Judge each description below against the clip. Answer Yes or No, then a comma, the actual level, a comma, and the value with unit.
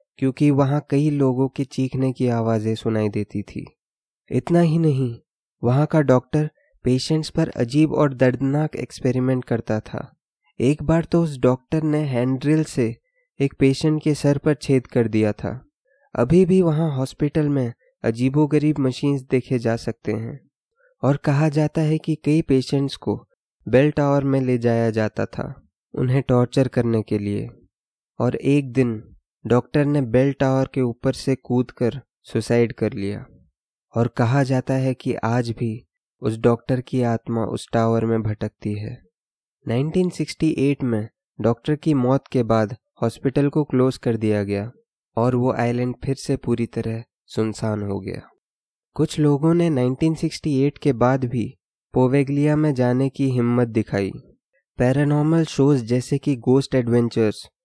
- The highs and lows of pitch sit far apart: No, average, 3.9 semitones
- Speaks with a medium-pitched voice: No, low, 130 Hz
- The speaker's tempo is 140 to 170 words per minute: Yes, average, 150 wpm